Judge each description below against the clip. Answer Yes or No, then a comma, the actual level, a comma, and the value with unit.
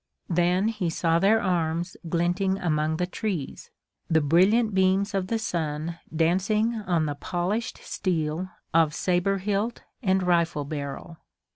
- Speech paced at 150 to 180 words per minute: No, slow, 135 wpm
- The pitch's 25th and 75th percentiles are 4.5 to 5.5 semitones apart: No, average, 3.2 semitones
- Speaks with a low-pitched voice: No, medium, 180 Hz